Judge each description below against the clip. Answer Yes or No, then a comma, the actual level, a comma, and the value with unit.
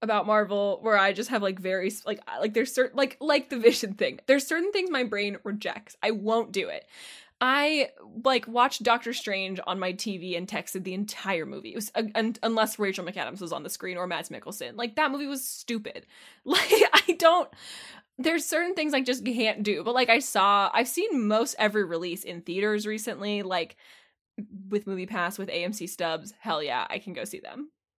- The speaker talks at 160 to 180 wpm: No, fast, 205 wpm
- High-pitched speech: Yes, high, 220 Hz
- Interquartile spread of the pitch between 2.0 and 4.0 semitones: No, average, 4.7 semitones